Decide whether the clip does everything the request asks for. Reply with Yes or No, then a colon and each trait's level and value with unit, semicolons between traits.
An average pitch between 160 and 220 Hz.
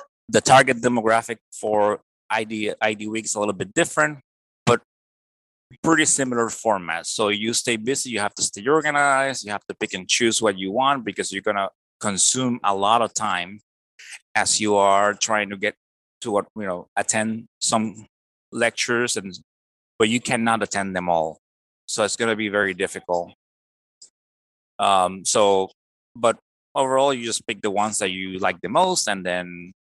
No: low, 105 Hz